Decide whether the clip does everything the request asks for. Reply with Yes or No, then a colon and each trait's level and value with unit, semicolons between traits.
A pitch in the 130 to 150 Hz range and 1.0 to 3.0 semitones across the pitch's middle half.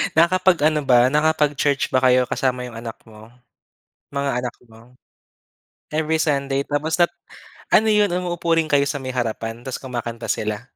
No: medium, 140 Hz; average, 4.3 semitones